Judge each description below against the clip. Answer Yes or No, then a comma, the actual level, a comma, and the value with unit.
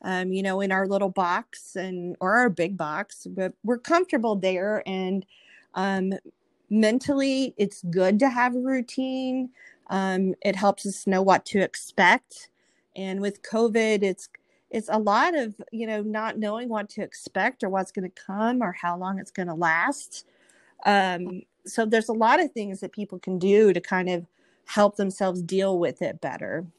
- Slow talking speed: No, average, 180 wpm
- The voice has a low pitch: No, high, 200 Hz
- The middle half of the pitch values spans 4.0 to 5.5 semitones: No, average, 3.3 semitones